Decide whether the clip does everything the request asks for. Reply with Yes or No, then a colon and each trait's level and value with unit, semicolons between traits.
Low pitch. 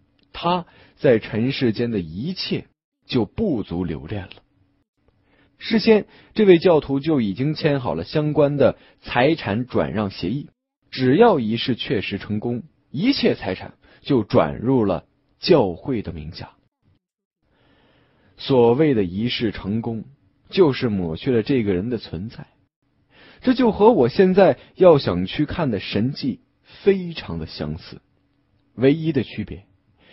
Yes: low, 125 Hz